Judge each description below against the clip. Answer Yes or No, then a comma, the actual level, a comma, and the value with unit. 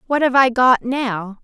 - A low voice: No, high, 245 Hz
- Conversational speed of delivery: No, fast, 210 wpm